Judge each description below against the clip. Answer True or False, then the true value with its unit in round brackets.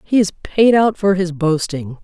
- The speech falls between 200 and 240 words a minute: True (205 wpm)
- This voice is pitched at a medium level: True (180 Hz)